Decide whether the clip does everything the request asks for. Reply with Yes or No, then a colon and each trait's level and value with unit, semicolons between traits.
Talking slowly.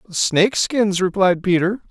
Yes: slow, 125 wpm